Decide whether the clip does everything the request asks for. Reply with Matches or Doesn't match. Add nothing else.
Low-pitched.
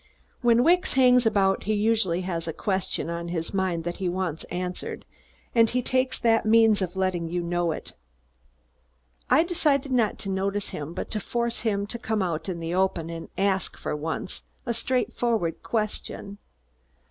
Doesn't match